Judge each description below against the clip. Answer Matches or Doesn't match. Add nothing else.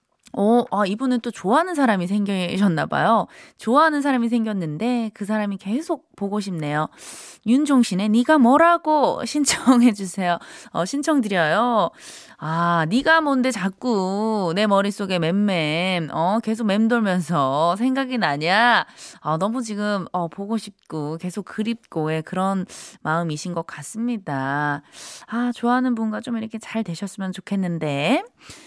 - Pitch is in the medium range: Doesn't match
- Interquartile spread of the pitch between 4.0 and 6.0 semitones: Matches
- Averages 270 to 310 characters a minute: Matches